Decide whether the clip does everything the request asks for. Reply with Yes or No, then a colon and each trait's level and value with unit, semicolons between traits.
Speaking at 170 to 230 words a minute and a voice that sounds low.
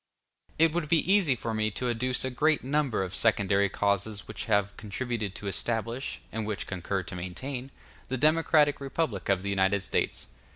Yes: average, 175 wpm; low, 115 Hz